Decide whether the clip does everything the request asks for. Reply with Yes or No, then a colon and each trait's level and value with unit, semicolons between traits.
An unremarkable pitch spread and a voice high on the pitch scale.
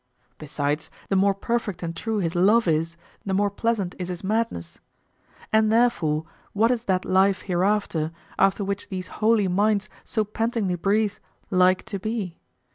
Yes: average, 3.4 semitones; high, 195 Hz